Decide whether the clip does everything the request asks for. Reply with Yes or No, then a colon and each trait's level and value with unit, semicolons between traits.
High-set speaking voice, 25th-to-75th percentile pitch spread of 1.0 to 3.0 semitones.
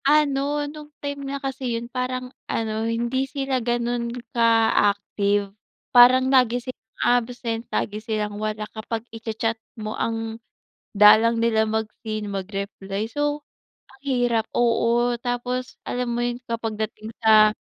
Yes: high, 235 Hz; narrow, 2.6 semitones